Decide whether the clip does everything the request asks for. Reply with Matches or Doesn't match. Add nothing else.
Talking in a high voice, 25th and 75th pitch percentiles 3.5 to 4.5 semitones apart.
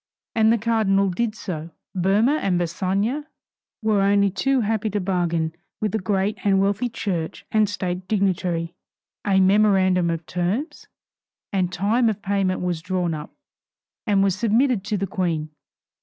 Doesn't match